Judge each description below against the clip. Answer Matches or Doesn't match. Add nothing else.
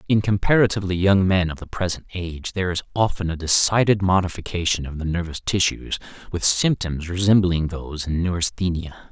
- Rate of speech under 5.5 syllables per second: Doesn't match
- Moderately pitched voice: Doesn't match